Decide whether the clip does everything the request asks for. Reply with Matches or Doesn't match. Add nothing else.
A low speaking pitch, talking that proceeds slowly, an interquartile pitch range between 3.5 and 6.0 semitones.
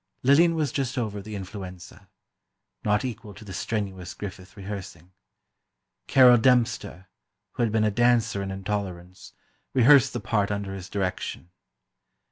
Matches